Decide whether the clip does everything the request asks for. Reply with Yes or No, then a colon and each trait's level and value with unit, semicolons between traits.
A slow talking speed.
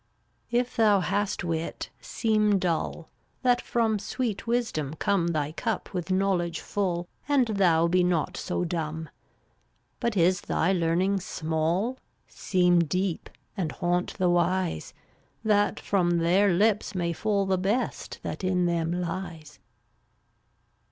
Yes: slow, 130 wpm